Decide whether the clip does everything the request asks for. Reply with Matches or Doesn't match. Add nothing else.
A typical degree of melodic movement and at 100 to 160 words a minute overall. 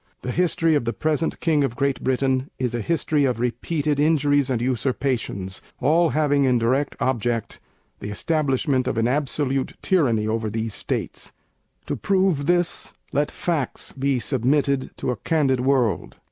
Matches